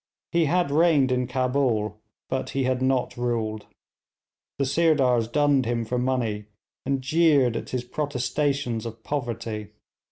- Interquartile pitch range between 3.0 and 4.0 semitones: Yes, average, 3.3 semitones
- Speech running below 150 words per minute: Yes, slow, 135 wpm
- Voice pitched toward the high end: No, low, 130 Hz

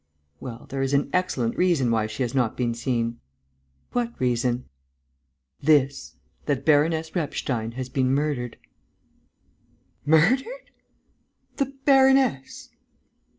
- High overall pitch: No, low, 135 Hz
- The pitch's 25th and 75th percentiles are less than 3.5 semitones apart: No, average, 5.0 semitones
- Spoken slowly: Yes, slow, 110 wpm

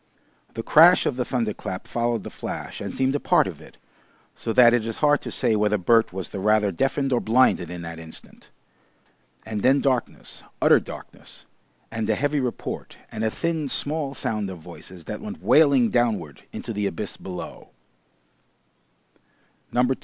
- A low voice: Yes, low, 115 Hz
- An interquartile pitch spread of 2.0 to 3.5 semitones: No, average, 4.7 semitones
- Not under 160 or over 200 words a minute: Yes, average, 170 wpm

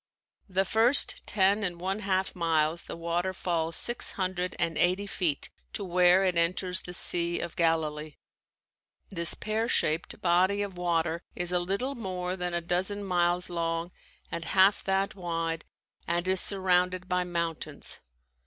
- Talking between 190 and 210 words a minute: No, average, 155 wpm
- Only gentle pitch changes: Yes, narrow, 2.0 semitones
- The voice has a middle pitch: Yes, medium, 180 Hz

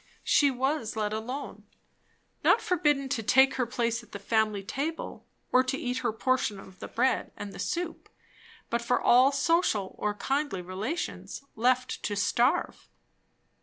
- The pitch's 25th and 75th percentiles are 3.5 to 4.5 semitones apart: Yes, average, 4.2 semitones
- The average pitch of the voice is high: Yes, very high, 250 Hz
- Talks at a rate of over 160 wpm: No, average, 155 wpm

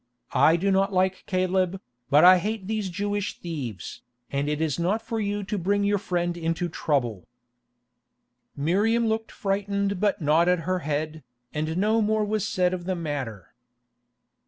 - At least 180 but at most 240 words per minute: No, average, 160 wpm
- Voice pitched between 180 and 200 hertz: Yes, medium, 185 Hz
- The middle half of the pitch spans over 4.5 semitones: No, average, 4.0 semitones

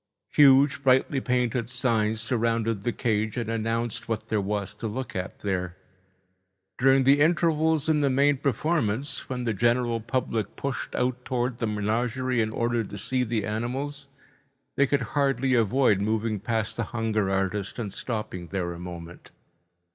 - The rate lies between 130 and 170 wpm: Yes, average, 155 wpm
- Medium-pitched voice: No, low, 115 Hz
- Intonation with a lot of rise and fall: No, average, 3.6 semitones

